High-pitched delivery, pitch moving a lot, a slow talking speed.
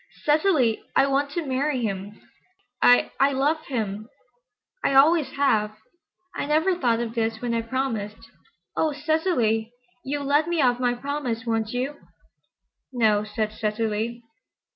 No: high, 245 Hz; average, 4.4 semitones; slow, 130 wpm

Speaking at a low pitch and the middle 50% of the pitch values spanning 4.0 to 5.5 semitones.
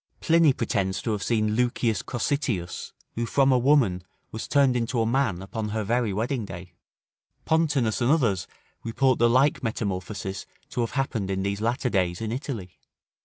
Yes: low, 115 Hz; average, 4.5 semitones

